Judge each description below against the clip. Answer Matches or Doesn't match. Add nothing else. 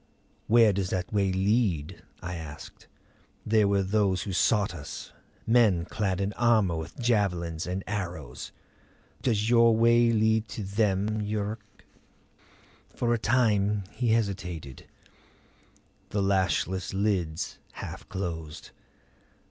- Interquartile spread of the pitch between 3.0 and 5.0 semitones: Matches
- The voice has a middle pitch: Doesn't match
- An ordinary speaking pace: Doesn't match